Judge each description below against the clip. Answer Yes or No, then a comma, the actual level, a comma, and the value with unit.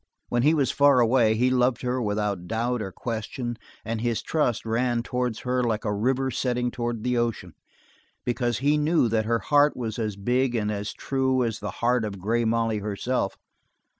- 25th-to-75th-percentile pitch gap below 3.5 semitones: Yes, narrow, 2.4 semitones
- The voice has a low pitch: Yes, low, 120 Hz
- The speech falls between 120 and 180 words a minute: No, average, 190 wpm